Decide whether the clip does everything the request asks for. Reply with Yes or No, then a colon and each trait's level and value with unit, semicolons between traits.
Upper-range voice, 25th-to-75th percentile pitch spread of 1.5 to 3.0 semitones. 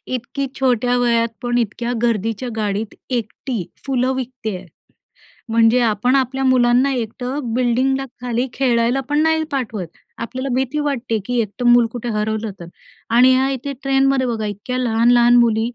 Yes: high, 245 Hz; narrow, 2.4 semitones